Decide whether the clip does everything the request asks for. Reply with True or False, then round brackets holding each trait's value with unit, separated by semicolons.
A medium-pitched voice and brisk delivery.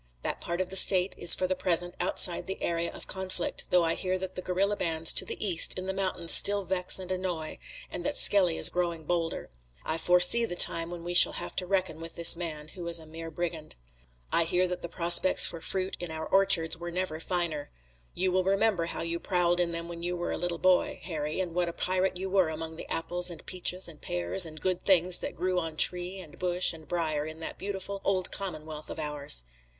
True (175 Hz; 230 wpm)